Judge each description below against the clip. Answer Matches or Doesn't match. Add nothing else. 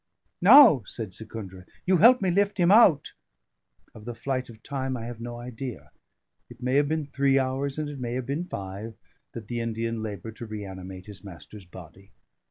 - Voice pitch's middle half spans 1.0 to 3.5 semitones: Doesn't match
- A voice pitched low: Matches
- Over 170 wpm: Matches